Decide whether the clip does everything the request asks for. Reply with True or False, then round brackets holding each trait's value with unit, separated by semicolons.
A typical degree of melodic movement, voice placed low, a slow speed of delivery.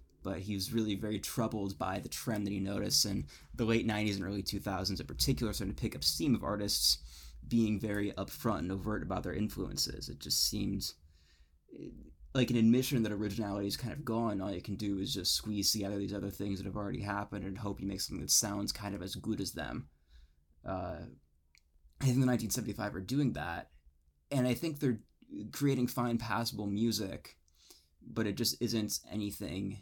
False (3.3 semitones; 100 Hz; 195 wpm)